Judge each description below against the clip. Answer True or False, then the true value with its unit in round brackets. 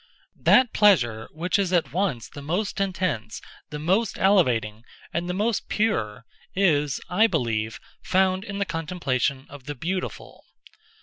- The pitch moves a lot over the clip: True (7.1 semitones)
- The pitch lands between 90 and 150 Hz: False (170 Hz)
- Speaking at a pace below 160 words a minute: True (140 wpm)